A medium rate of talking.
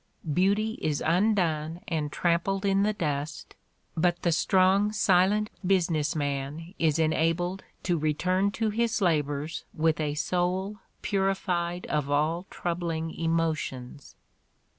No: slow, 120 wpm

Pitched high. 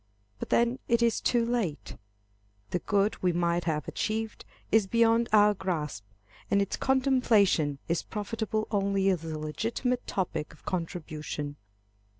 Yes: high, 200 Hz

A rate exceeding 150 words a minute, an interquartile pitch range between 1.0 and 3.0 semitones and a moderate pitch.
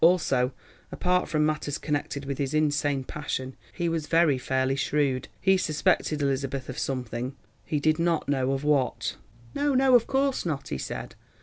No: average, 170 wpm; average, 3.5 semitones; medium, 145 Hz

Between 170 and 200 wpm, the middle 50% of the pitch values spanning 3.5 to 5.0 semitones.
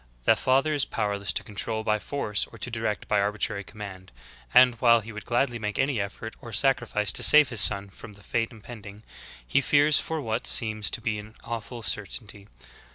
No: average, 195 wpm; average, 2.9 semitones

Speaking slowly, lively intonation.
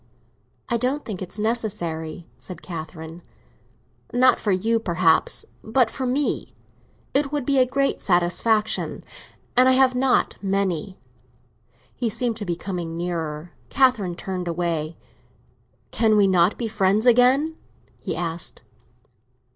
Yes: slow, 130 wpm; wide, 6.2 semitones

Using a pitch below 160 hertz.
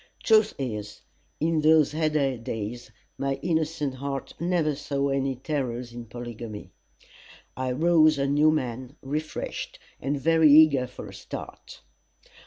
Yes: medium, 140 Hz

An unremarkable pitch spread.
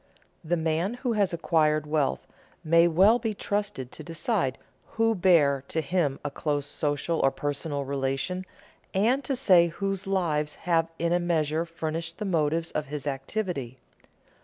Yes: average, 4.2 semitones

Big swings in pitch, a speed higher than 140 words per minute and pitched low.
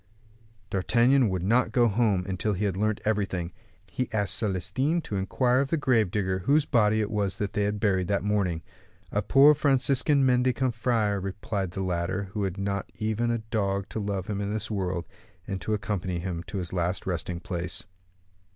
No: average, 3.7 semitones; average, 185 wpm; low, 100 Hz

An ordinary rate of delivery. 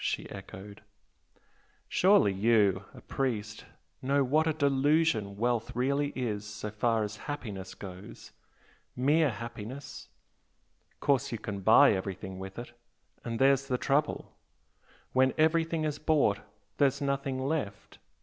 No: slow, 125 wpm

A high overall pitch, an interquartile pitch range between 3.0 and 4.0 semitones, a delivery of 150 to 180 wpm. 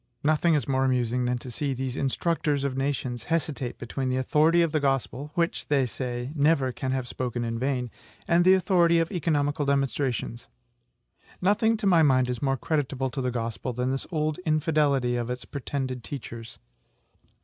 No: low, 135 Hz; average, 3.6 semitones; average, 175 wpm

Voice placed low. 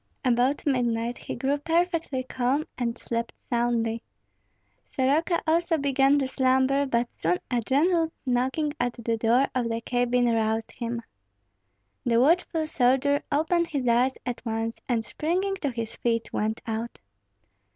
No: very high, 250 Hz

